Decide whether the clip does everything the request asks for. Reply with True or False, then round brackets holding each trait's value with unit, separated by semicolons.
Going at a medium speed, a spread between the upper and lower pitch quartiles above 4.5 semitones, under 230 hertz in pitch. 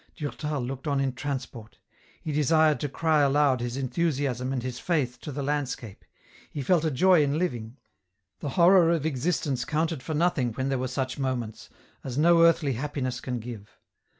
False (180 wpm; 3.5 semitones; 140 Hz)